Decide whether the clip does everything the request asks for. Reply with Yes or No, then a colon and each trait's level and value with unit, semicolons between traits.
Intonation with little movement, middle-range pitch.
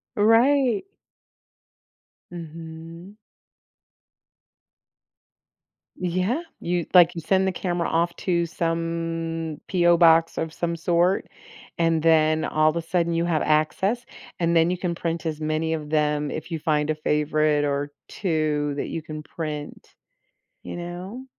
Yes: narrow, 2.0 semitones; medium, 165 Hz